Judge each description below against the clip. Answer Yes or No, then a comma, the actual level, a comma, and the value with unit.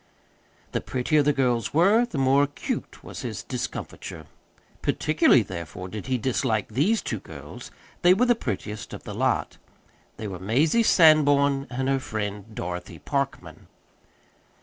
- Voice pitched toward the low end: Yes, low, 130 Hz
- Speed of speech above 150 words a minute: No, average, 145 wpm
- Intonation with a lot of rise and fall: Yes, wide, 6.0 semitones